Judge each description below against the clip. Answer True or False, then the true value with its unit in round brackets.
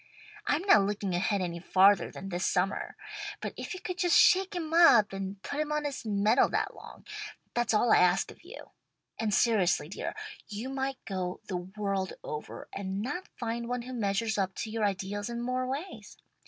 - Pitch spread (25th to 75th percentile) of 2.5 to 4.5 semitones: False (5.2 semitones)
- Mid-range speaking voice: False (215 Hz)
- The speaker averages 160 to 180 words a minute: False (195 wpm)